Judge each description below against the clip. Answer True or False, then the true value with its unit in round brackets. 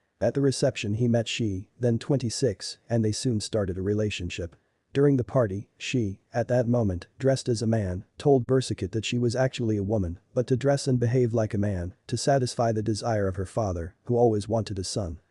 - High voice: False (115 Hz)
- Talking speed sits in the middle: False (210 wpm)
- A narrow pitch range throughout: False (3.7 semitones)